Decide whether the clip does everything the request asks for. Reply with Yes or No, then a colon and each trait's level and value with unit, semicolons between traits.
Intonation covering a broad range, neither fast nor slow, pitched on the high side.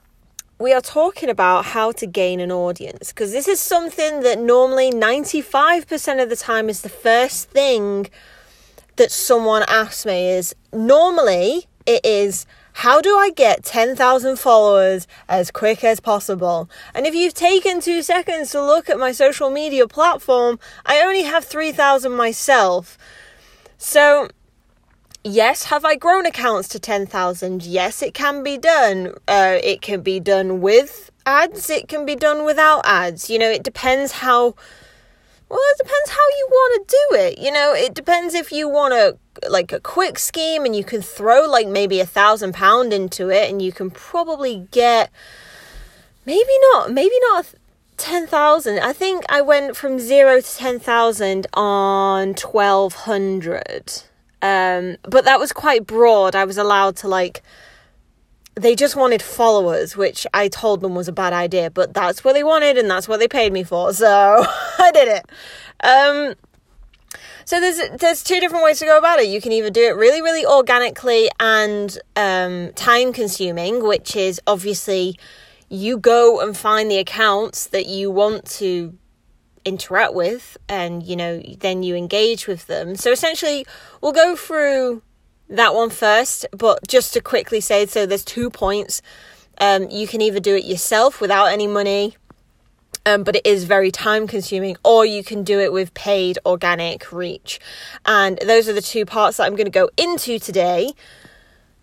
Yes: wide, 7.0 semitones; average, 170 wpm; high, 225 Hz